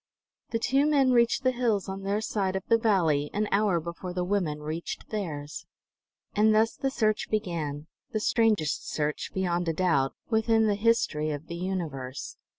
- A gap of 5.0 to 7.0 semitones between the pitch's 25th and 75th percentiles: Yes, wide, 5.5 semitones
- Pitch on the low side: No, high, 190 Hz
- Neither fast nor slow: Yes, average, 170 wpm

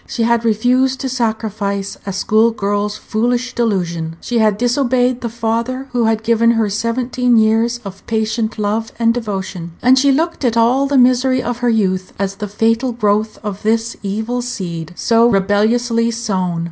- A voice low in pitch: No, high, 225 Hz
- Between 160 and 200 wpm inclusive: Yes, average, 170 wpm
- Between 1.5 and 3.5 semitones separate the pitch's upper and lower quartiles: Yes, average, 2.8 semitones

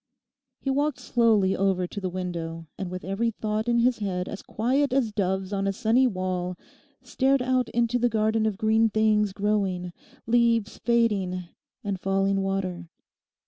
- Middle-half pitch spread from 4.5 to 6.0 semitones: No, average, 3.7 semitones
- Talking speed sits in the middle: Yes, average, 160 wpm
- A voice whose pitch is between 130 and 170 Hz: No, high, 210 Hz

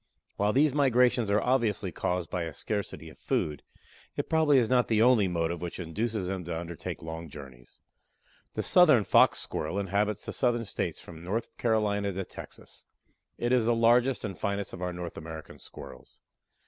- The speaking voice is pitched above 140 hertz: No, low, 100 Hz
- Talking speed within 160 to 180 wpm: Yes, average, 175 wpm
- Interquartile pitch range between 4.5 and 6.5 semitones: Yes, wide, 5.5 semitones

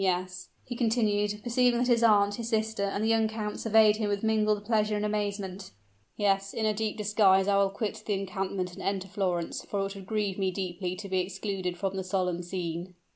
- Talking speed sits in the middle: No, fast, 210 wpm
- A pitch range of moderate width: No, narrow, 2.2 semitones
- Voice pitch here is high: Yes, high, 200 Hz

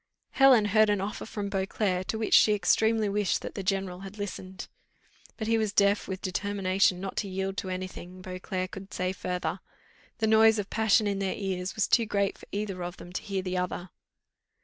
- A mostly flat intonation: Yes, narrow, 2.1 semitones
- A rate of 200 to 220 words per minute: Yes, fast, 205 wpm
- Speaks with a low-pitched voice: No, high, 195 Hz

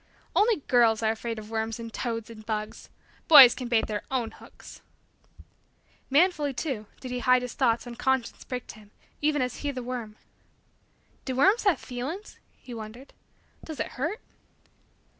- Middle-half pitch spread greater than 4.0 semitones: No, average, 3.6 semitones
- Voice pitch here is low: No, very high, 250 Hz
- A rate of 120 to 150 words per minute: No, average, 160 wpm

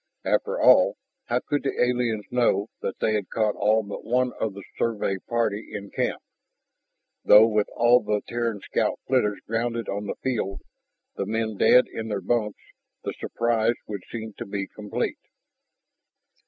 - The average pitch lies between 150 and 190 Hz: No, low, 110 Hz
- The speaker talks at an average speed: Yes, average, 160 wpm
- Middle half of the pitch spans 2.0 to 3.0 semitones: Yes, narrow, 2.4 semitones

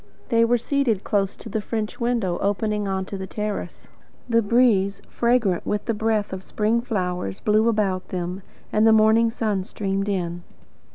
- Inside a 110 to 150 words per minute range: No, average, 170 wpm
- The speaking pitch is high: Yes, high, 210 Hz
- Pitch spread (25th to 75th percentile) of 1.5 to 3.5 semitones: Yes, average, 2.9 semitones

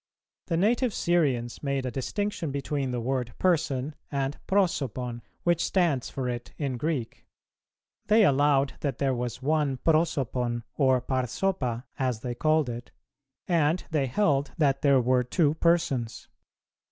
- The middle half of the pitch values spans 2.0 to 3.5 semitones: No, average, 4.3 semitones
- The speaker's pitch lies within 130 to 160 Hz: Yes, medium, 140 Hz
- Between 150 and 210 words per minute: No, slow, 135 wpm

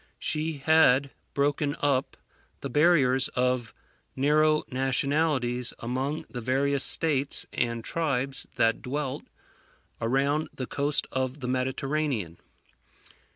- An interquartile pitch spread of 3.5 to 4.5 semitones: No, narrow, 2.6 semitones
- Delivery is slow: Yes, slow, 105 wpm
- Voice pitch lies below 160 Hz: Yes, low, 135 Hz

